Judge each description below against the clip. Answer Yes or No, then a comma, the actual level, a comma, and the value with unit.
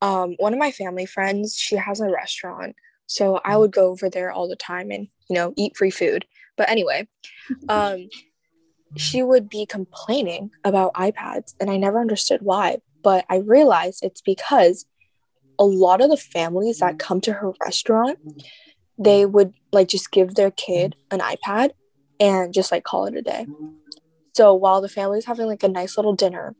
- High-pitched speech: Yes, high, 195 Hz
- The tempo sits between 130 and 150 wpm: No, average, 180 wpm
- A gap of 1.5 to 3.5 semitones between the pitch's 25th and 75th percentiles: Yes, average, 2.7 semitones